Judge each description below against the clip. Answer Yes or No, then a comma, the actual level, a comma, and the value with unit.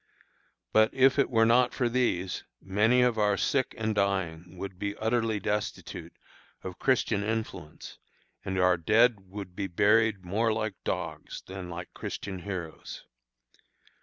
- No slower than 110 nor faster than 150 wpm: Yes, average, 140 wpm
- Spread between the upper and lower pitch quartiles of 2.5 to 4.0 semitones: Yes, average, 3.4 semitones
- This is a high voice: No, low, 100 Hz